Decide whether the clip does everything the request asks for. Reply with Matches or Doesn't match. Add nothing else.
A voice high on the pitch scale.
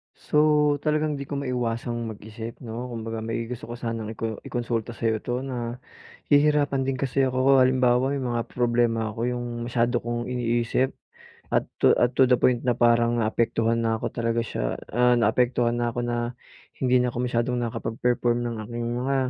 Doesn't match